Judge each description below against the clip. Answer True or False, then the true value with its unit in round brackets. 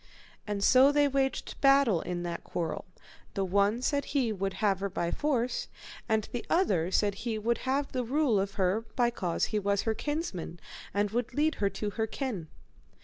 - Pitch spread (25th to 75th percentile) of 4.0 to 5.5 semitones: True (5.2 semitones)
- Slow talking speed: False (190 wpm)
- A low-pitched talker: False (220 Hz)